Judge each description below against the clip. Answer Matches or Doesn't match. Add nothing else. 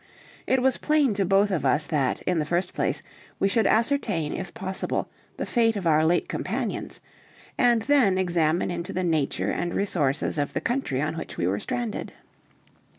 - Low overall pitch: Doesn't match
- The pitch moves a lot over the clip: Matches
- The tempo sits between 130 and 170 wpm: Doesn't match